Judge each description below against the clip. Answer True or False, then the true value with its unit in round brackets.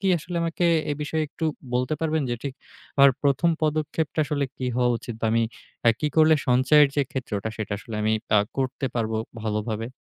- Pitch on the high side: False (140 Hz)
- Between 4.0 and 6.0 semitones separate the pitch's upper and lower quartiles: True (4.9 semitones)